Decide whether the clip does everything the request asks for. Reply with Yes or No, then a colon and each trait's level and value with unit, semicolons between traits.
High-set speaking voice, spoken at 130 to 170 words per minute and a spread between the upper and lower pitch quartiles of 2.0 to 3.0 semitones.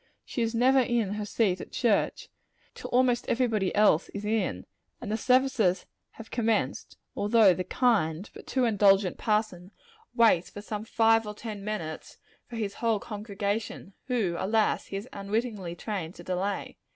Yes: high, 210 Hz; average, 160 wpm; average, 2.7 semitones